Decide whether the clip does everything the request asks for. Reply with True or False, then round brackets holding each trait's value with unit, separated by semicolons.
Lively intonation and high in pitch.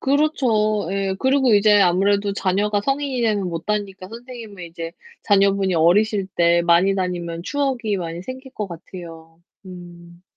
False (4.0 semitones; 195 Hz)